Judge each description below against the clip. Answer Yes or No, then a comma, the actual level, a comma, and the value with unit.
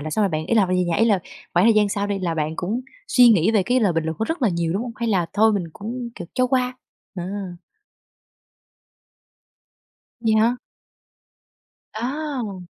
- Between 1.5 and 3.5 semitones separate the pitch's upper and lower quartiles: No, average, 4.8 semitones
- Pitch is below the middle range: No, high, 210 Hz